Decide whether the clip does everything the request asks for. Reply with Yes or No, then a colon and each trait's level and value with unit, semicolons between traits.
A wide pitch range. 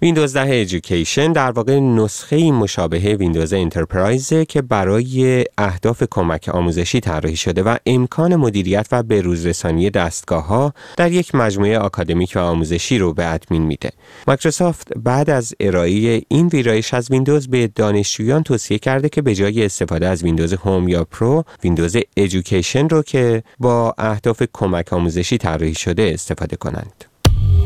Yes: wide, 6.5 semitones